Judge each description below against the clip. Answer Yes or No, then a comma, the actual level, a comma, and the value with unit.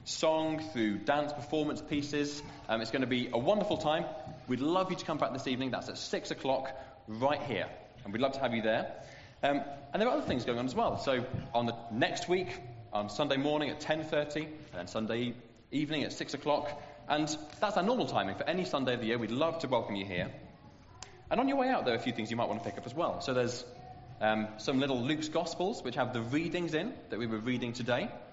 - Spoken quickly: Yes, fast, 240 wpm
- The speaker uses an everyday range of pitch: Yes, average, 4.0 semitones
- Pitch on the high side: No, medium, 140 Hz